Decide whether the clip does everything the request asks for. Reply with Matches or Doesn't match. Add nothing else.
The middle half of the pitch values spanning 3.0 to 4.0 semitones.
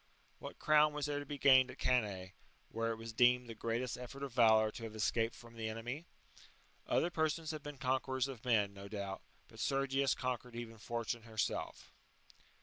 Matches